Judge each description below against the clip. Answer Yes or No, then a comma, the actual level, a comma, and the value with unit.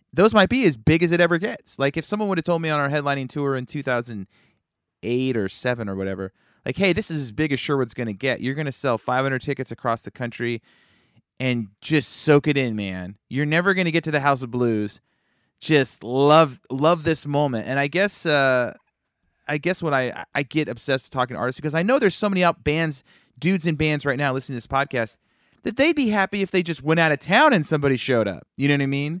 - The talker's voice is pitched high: No, medium, 140 Hz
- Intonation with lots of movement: No, average, 4.7 semitones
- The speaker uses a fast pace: Yes, fast, 240 wpm